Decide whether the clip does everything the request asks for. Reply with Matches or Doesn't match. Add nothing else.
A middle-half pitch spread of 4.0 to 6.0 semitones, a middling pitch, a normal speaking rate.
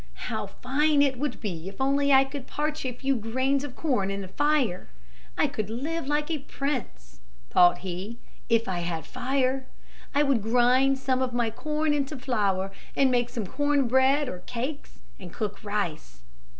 Doesn't match